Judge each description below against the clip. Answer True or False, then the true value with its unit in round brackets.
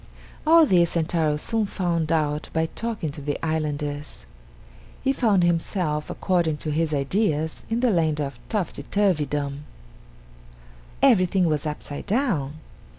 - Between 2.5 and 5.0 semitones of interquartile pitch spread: True (4.3 semitones)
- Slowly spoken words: True (130 wpm)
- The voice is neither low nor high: True (160 Hz)